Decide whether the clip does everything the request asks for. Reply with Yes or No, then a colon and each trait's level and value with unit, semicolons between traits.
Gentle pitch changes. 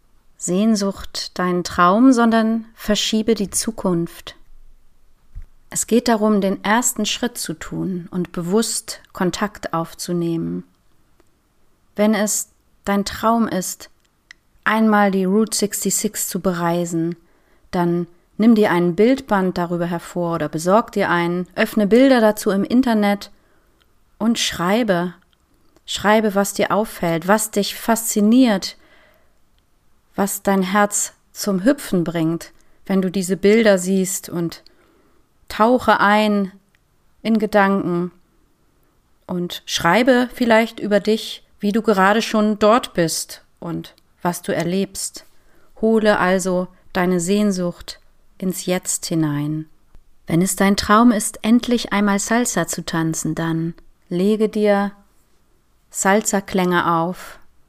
No: average, 3.6 semitones